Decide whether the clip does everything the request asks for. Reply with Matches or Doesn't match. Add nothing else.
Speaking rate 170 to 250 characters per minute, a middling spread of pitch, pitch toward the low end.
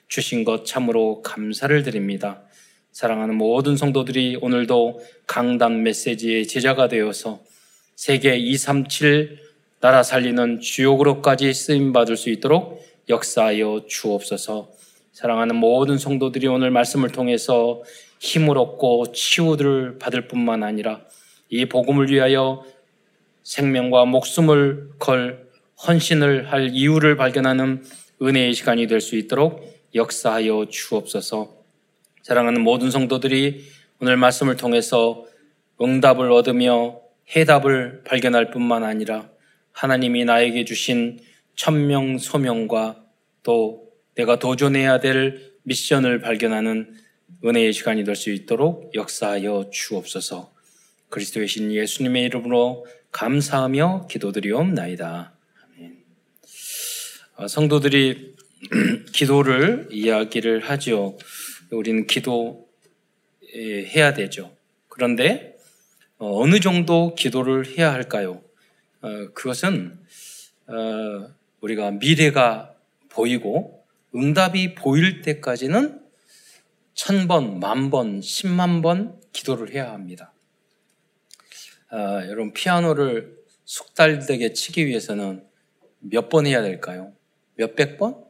Matches